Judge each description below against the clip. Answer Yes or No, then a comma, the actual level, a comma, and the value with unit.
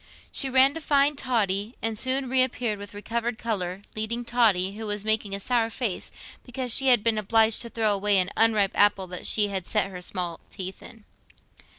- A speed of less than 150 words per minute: No, average, 195 wpm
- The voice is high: Yes, high, 220 Hz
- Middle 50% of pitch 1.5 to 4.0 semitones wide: Yes, average, 3.4 semitones